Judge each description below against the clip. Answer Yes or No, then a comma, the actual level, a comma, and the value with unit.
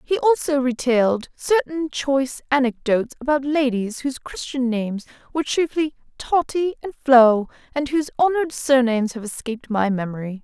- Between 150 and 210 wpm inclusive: No, average, 140 wpm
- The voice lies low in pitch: No, very high, 265 Hz